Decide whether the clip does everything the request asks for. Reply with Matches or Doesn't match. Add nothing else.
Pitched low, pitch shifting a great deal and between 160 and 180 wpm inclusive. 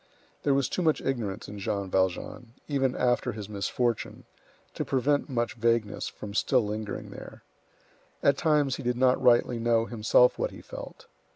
Doesn't match